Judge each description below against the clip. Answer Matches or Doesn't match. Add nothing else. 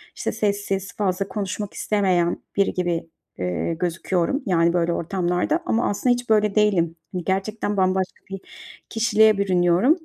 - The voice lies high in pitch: Matches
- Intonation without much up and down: Doesn't match